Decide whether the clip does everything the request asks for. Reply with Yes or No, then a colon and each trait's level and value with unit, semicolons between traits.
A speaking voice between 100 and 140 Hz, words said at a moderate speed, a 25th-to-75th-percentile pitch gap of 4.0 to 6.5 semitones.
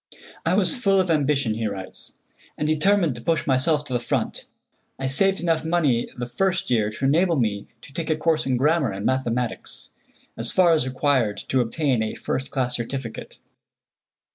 Yes: low, 135 Hz; average, 180 wpm; average, 5.3 semitones